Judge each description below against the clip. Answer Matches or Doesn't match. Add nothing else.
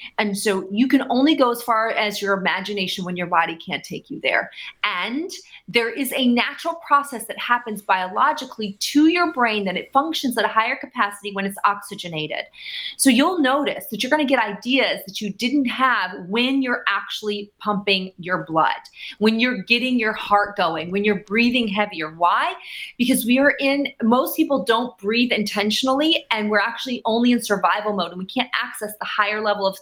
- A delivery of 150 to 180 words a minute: Doesn't match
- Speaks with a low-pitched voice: Doesn't match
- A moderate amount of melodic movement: Matches